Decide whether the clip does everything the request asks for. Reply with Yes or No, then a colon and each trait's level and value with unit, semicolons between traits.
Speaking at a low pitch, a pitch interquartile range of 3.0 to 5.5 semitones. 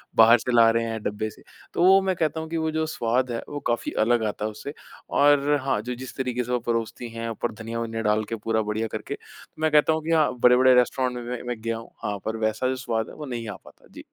Yes: low, 120 Hz; average, 3.7 semitones